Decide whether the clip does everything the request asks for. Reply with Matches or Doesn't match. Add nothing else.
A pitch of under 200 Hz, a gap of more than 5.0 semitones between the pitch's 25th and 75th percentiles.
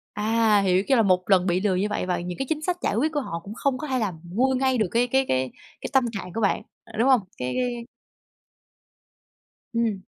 Doesn't match